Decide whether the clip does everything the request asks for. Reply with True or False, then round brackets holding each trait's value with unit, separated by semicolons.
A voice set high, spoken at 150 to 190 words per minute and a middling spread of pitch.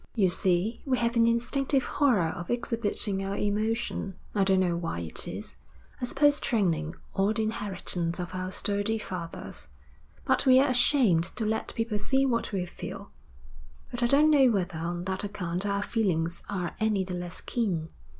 True (205 Hz; 170 wpm; 4.6 semitones)